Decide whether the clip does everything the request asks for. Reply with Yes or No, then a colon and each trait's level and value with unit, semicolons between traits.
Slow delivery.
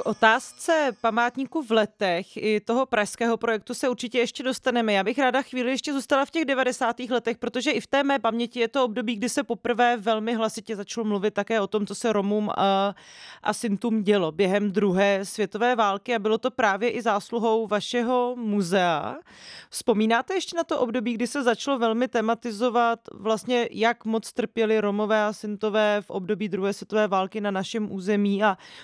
No: average, 180 wpm